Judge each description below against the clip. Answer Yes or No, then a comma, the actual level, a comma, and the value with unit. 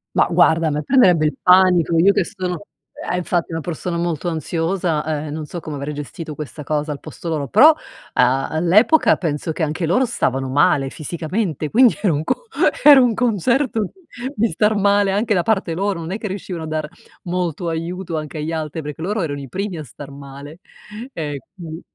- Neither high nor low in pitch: Yes, medium, 165 Hz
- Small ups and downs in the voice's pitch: No, average, 4.2 semitones